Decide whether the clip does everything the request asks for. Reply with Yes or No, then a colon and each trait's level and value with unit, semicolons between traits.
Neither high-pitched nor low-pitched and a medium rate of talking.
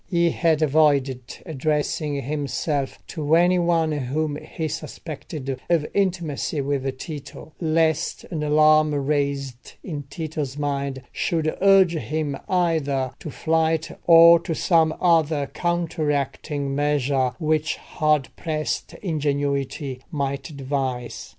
No: medium, 150 Hz; slow, 110 wpm